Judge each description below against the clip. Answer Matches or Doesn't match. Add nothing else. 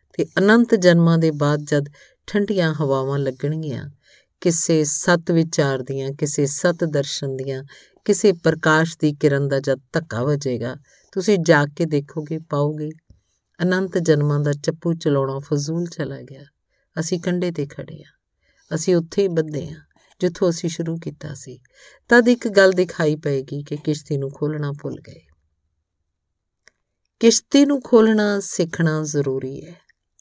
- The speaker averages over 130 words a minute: Matches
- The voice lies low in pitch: Doesn't match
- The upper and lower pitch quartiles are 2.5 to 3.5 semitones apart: Doesn't match